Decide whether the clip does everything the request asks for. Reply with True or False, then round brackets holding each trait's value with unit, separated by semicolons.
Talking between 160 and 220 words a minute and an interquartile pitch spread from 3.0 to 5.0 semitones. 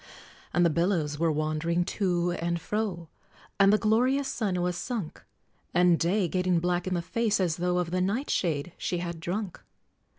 False (170 wpm; 2.6 semitones)